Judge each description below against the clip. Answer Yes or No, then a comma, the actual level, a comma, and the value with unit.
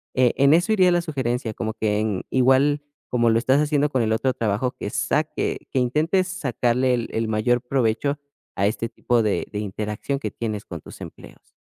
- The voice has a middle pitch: No, low, 125 Hz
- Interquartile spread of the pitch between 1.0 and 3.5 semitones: No, average, 4.2 semitones